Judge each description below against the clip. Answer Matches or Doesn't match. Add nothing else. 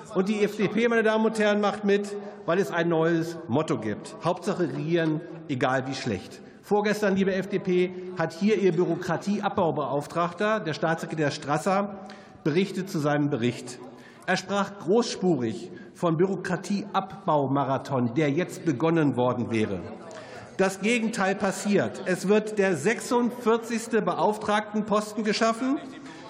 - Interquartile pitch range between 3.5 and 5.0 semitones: Matches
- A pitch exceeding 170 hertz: Matches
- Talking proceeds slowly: Matches